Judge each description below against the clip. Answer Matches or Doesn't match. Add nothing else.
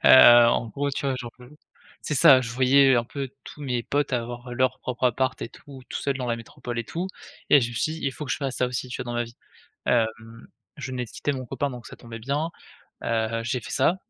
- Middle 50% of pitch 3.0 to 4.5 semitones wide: Doesn't match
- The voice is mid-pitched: Doesn't match